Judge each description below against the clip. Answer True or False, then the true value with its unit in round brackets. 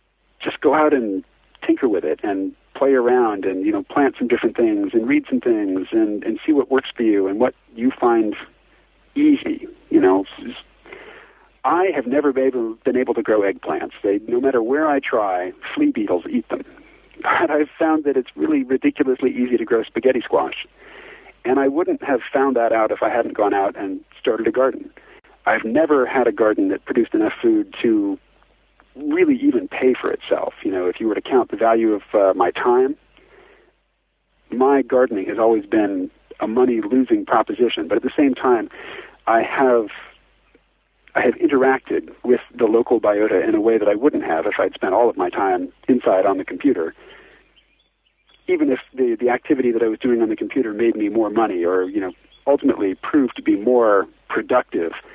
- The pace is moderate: True (195 wpm)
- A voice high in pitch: True (315 Hz)